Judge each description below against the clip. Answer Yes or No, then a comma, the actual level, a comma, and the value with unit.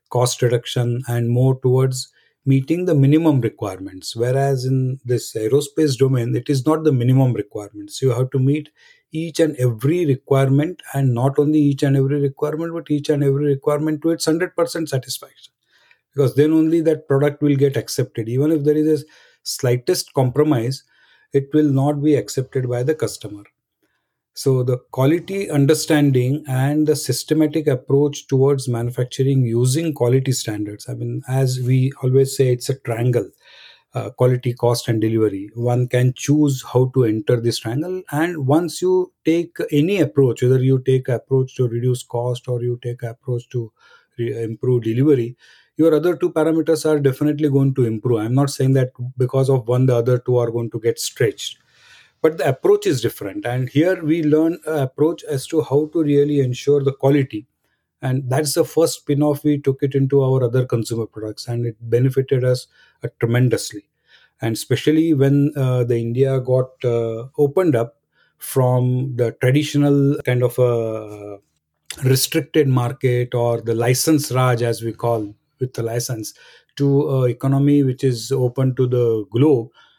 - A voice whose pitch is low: Yes, low, 130 Hz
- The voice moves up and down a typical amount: Yes, average, 3.3 semitones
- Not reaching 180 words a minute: Yes, average, 165 wpm